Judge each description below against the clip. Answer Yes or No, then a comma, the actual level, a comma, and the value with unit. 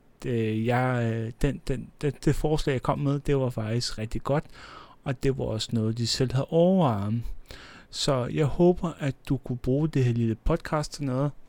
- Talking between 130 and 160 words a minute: No, average, 190 wpm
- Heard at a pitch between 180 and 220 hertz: No, low, 135 Hz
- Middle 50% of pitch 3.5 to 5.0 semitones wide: Yes, average, 4.0 semitones